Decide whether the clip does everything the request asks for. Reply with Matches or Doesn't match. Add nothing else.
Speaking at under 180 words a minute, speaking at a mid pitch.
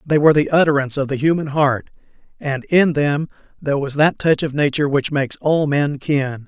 Doesn't match